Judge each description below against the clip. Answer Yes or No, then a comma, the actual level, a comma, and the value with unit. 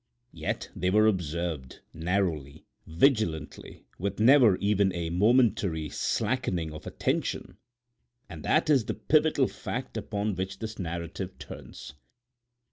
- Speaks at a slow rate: Yes, slow, 120 wpm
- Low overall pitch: Yes, very low, 95 Hz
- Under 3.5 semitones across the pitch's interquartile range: No, average, 4.7 semitones